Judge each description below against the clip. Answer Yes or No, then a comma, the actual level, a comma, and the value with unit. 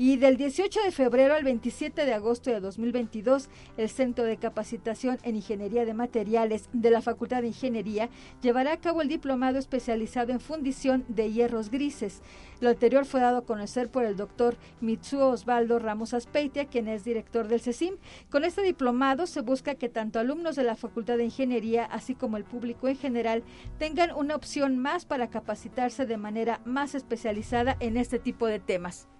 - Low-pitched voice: No, high, 245 Hz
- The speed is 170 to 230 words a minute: Yes, average, 180 wpm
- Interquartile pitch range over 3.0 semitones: No, average, 2.7 semitones